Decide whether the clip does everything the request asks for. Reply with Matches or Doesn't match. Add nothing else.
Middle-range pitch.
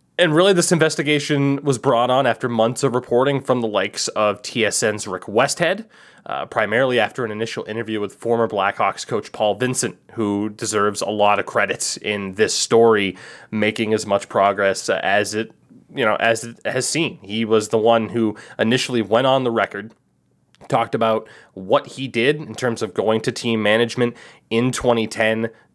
Doesn't match